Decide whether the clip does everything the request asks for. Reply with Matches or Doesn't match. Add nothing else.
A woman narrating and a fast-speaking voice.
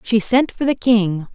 Matches